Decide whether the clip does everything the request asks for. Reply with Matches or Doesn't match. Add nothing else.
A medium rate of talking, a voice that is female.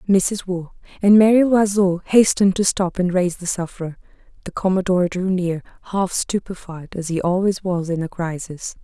Matches